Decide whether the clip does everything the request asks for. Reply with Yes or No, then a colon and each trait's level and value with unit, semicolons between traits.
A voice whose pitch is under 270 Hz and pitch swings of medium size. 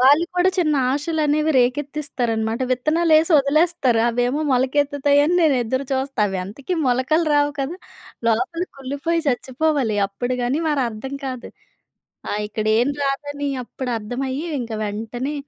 No: very high, 275 Hz; average, 3.5 semitones